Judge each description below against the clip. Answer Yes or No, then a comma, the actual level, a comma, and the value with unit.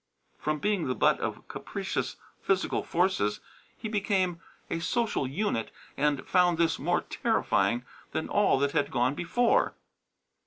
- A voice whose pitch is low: No, medium, 165 Hz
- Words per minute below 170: Yes, average, 140 wpm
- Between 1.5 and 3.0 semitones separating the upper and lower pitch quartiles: No, wide, 5.6 semitones